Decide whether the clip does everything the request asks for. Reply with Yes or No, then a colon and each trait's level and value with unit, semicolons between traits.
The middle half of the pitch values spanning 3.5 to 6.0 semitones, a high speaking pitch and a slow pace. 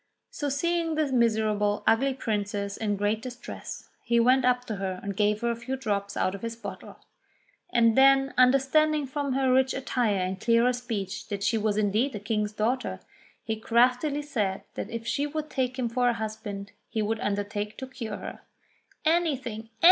No: average, 4.0 semitones; high, 230 Hz; average, 180 wpm